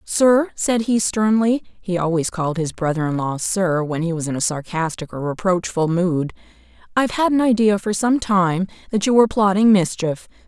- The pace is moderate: Yes, average, 180 wpm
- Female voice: Yes, female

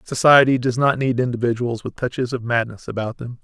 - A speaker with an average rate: Yes, average, 190 wpm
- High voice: No, low, 120 Hz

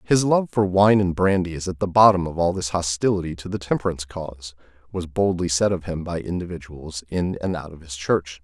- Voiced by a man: Yes, male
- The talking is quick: Yes, fast, 220 wpm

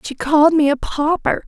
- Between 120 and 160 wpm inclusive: No, fast, 205 wpm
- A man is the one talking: No, female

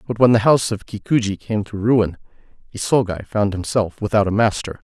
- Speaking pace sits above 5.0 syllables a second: Yes, 5.6 syllables/s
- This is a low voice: Yes, low, 105 Hz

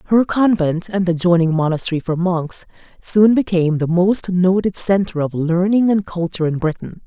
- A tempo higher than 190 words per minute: No, average, 160 wpm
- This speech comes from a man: No, female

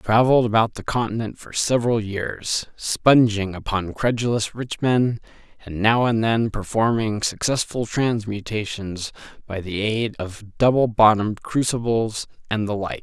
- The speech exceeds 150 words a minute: No, average, 140 wpm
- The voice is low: Yes, low, 110 Hz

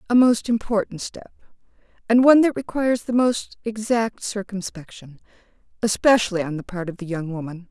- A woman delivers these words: Yes, female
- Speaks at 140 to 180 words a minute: Yes, average, 150 wpm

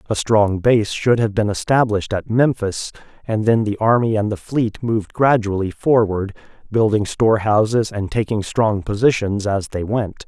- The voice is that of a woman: No, male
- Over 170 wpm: No, average, 165 wpm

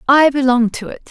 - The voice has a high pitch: Yes, very high, 260 Hz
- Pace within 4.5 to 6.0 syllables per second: Yes, 5.3 syllables/s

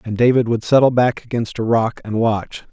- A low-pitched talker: Yes, low, 115 Hz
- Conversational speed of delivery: No, fast, 220 wpm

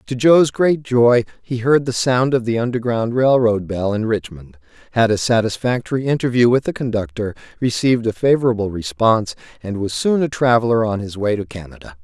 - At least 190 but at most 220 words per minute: No, average, 175 wpm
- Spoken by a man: Yes, male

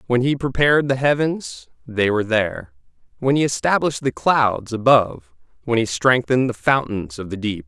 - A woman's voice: No, male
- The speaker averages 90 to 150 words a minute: No, average, 170 wpm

